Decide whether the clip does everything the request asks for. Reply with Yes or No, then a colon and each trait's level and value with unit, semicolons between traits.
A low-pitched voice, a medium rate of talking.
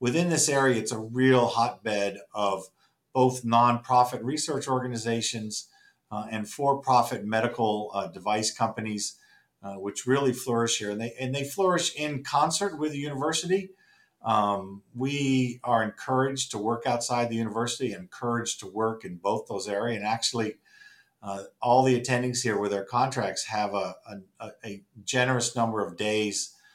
Yes: low, 120 Hz; average, 155 wpm